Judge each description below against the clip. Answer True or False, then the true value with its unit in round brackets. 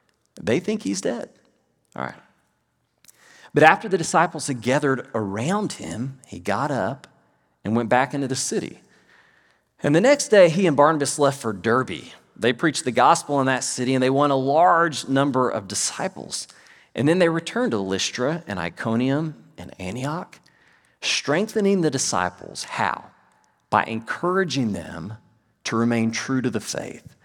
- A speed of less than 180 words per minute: True (155 wpm)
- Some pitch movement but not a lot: False (5.9 semitones)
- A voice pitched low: True (130 Hz)